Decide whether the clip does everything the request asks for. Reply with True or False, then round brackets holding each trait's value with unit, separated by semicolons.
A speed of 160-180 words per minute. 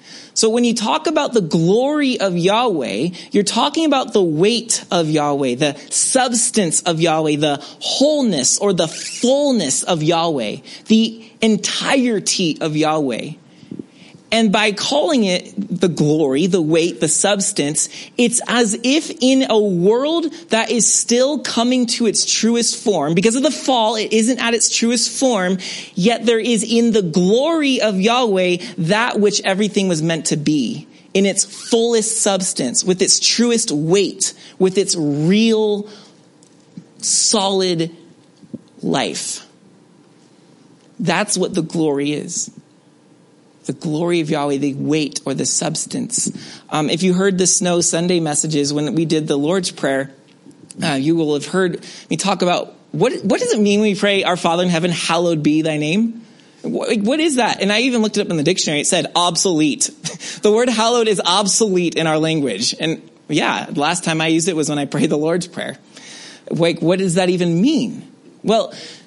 True (165 wpm)